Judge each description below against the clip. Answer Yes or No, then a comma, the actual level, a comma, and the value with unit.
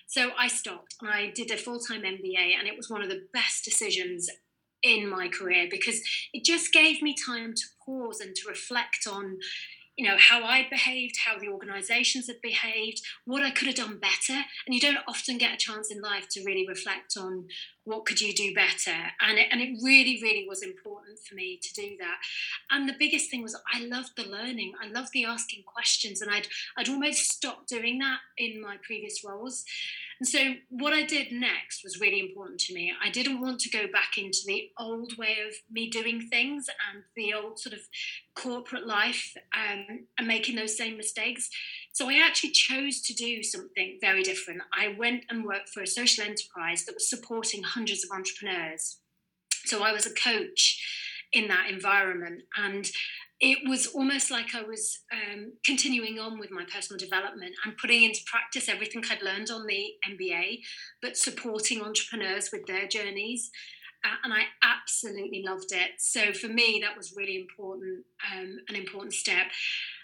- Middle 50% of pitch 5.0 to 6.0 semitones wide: No, average, 4.3 semitones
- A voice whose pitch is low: No, high, 230 Hz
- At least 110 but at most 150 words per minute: No, average, 190 wpm